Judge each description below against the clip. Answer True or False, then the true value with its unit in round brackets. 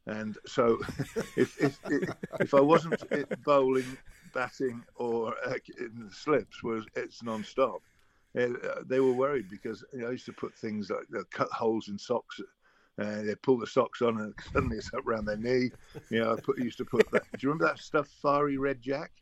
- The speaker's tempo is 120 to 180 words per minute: False (200 wpm)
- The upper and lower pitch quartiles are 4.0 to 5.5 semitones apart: False (3.4 semitones)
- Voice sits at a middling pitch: False (120 Hz)